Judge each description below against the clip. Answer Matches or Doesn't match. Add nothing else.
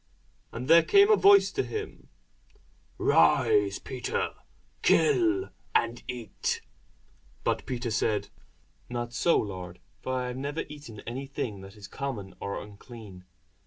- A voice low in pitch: Matches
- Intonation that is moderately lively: Doesn't match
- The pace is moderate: Doesn't match